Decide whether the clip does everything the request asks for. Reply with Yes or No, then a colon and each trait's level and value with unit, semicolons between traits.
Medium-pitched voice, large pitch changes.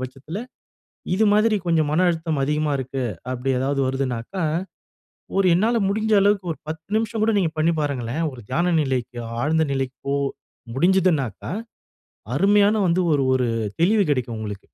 Yes: medium, 155 Hz; wide, 6.3 semitones